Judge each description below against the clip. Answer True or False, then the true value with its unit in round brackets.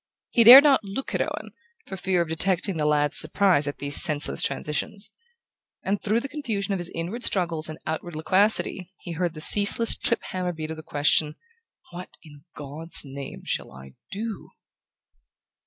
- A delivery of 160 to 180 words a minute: True (170 wpm)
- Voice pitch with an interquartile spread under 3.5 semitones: False (4.6 semitones)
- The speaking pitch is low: False (175 Hz)